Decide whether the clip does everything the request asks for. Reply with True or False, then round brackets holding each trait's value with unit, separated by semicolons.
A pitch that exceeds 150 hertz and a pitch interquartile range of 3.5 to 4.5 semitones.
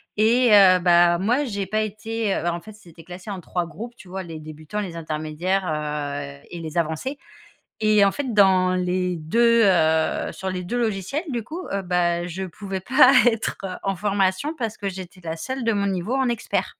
True (190 Hz; 4.0 semitones)